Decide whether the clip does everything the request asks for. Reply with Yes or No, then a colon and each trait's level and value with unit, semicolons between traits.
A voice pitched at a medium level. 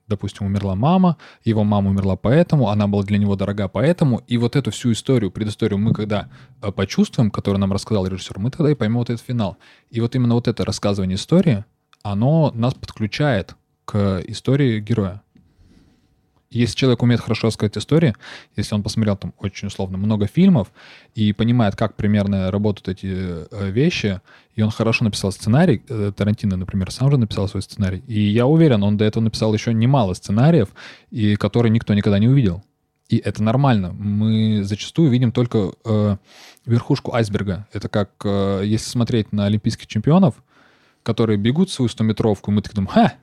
No: low, 110 Hz